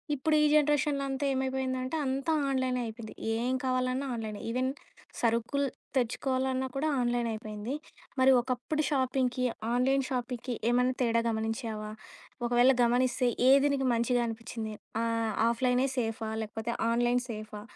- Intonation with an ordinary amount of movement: No, narrow, 2.3 semitones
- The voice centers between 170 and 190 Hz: No, very high, 250 Hz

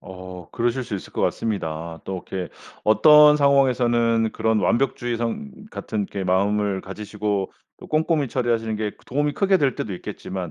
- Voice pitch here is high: No, low, 110 Hz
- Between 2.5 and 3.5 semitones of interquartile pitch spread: No, average, 4.9 semitones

